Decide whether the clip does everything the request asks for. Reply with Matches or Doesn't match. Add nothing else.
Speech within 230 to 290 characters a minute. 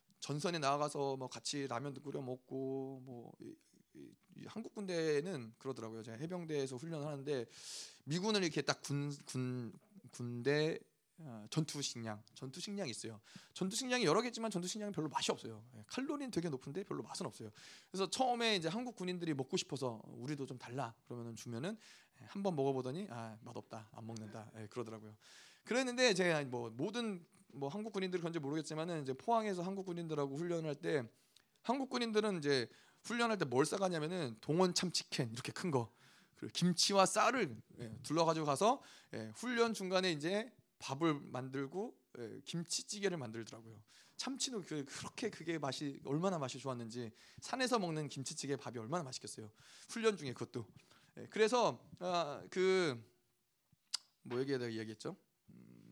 Doesn't match